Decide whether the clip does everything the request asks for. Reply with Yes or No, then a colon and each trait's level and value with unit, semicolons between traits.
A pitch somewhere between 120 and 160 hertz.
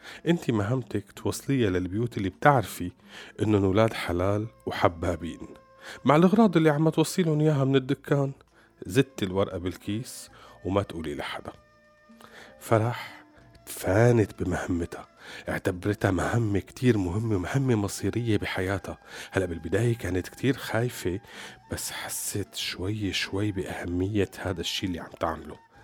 No: low, 105 Hz